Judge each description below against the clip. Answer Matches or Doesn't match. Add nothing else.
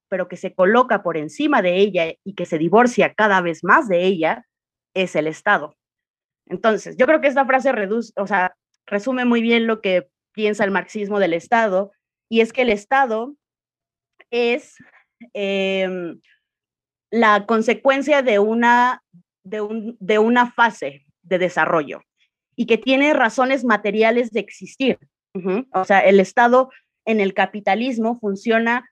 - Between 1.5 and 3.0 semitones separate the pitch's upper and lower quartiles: Doesn't match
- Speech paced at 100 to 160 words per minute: Matches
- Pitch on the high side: Matches